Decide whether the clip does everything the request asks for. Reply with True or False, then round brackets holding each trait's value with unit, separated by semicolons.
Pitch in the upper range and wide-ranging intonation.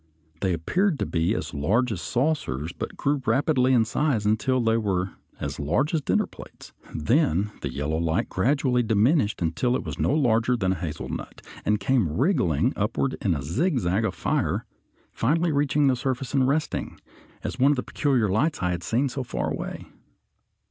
False (120 Hz; 6.9 semitones)